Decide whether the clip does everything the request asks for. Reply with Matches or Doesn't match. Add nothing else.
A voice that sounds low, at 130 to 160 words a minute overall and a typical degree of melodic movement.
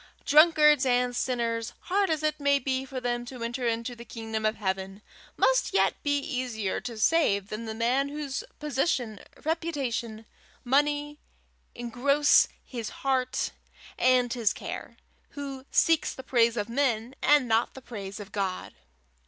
Doesn't match